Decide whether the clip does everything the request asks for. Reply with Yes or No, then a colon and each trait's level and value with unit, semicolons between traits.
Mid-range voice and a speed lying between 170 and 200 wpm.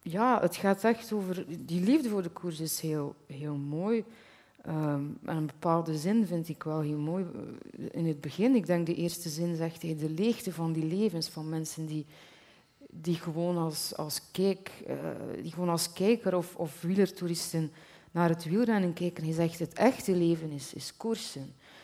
Yes: medium, 170 Hz; average, 185 wpm